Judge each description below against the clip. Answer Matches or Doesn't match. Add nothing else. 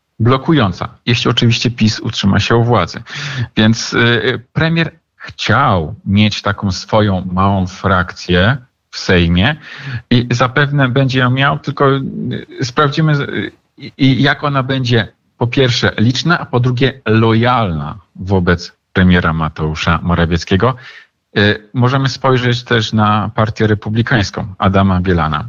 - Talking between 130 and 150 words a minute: Doesn't match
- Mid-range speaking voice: Doesn't match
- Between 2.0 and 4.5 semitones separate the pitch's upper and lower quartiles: Doesn't match